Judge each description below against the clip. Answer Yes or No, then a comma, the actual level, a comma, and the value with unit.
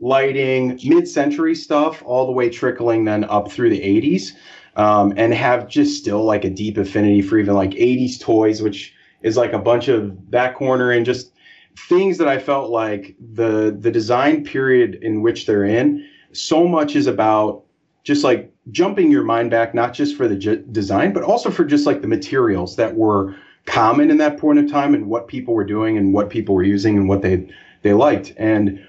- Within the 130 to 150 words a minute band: No, average, 200 wpm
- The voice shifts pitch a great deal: Yes, wide, 6.9 semitones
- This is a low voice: Yes, low, 120 Hz